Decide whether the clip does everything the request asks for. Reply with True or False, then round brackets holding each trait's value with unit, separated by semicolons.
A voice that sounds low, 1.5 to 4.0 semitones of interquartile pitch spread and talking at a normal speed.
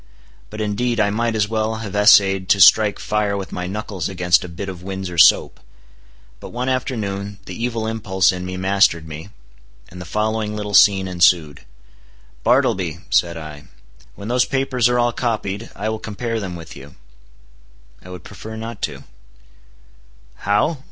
True (100 Hz; 3.4 semitones; 165 wpm)